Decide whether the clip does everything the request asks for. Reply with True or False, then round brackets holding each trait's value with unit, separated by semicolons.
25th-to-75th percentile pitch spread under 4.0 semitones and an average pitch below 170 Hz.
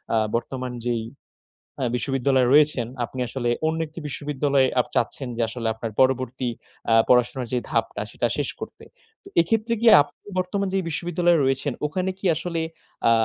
False (4.8 semitones; 135 Hz)